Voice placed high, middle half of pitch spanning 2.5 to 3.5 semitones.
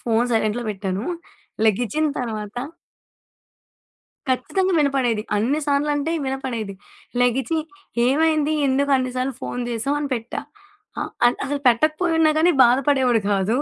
No: very high, 255 Hz; average, 4.1 semitones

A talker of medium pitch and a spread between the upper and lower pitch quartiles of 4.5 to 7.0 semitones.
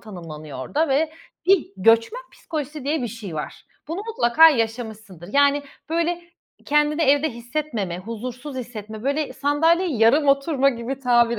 No: very high, 265 Hz; average, 5.1 semitones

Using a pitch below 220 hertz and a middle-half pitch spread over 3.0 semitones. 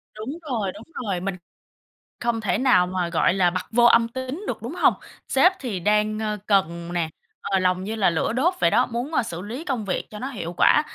Yes: high, 210 Hz; average, 4.8 semitones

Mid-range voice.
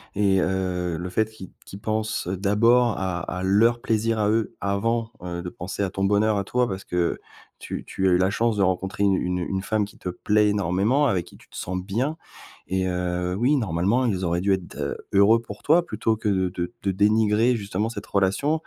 No: low, 100 Hz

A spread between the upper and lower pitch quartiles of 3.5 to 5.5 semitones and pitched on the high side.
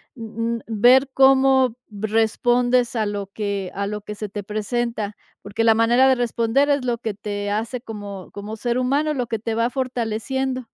No: average, 3.1 semitones; high, 230 Hz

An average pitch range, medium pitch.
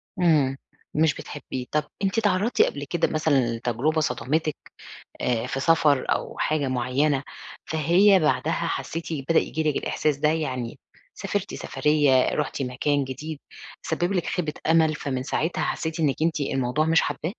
Yes: average, 3.2 semitones; medium, 150 Hz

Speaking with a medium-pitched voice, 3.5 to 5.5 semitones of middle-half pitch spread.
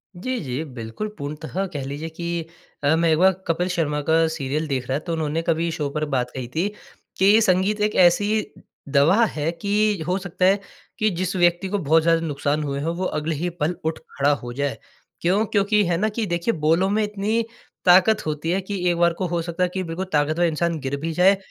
Yes: medium, 170 Hz; average, 3.8 semitones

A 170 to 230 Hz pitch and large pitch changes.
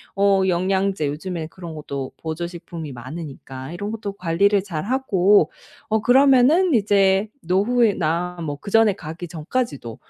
No: medium, 185 Hz; average, 4.4 semitones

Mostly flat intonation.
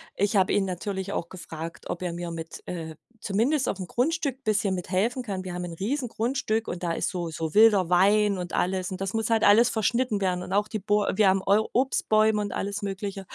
No: average, 3.2 semitones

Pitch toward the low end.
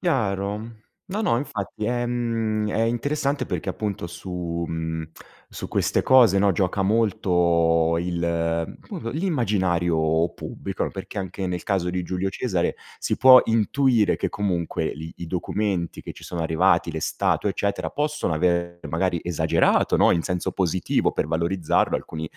Yes: very low, 95 Hz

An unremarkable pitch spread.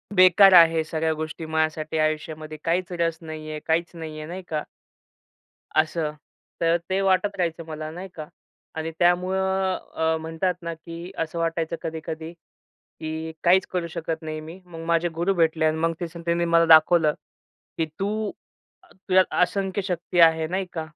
No: narrow, 2.1 semitones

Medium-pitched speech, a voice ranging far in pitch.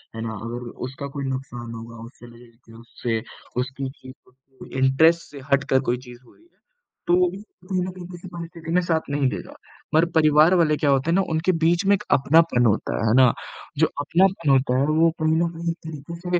No: medium, 145 Hz; average, 4.8 semitones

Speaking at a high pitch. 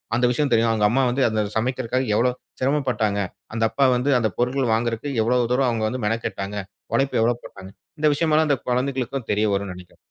No: low, 120 Hz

